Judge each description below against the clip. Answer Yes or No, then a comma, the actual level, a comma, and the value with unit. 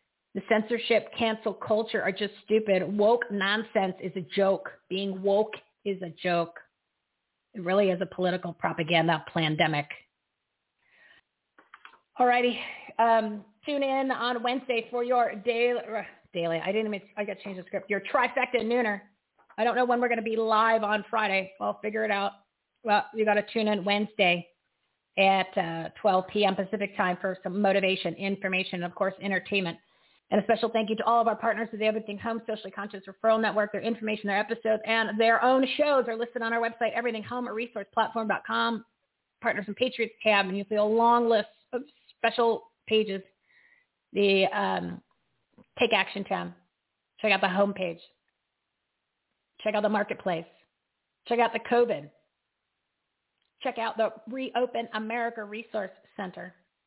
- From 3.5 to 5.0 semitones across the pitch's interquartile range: No, average, 2.9 semitones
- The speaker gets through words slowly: No, average, 165 wpm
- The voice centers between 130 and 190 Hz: No, high, 215 Hz